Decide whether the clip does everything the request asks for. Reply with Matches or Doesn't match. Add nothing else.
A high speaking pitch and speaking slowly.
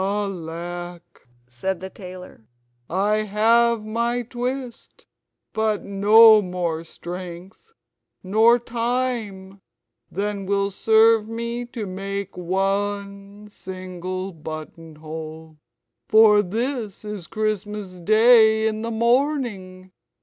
Matches